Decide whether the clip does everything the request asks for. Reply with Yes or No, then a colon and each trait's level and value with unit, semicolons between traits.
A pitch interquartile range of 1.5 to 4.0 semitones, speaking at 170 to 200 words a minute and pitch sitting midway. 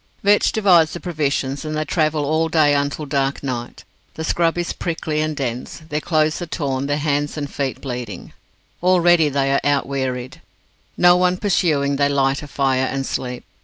Yes: average, 2.8 semitones; average, 185 wpm; medium, 145 Hz